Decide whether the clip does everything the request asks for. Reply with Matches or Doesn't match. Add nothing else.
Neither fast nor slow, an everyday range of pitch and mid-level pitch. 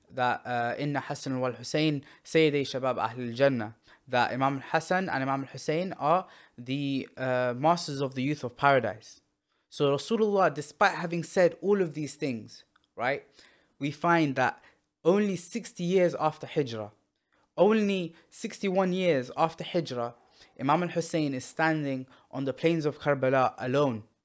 Matches